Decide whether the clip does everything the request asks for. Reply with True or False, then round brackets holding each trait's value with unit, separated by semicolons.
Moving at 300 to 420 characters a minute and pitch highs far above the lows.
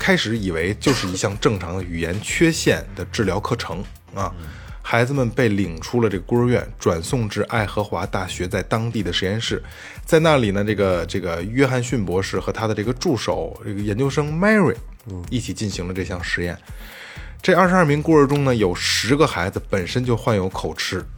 False (305 characters per minute; 5.0 semitones)